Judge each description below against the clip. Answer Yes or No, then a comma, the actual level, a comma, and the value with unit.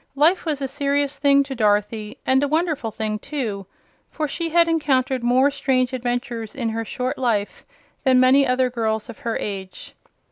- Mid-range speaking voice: No, very high, 255 Hz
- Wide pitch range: No, average, 3.7 semitones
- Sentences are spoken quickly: No, average, 175 wpm